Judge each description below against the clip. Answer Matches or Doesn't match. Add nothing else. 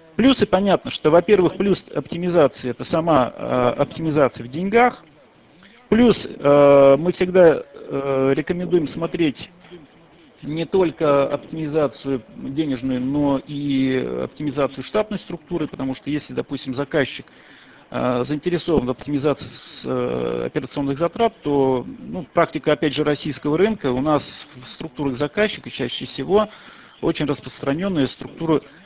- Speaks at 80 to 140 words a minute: Matches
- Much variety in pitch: Doesn't match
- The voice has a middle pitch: Matches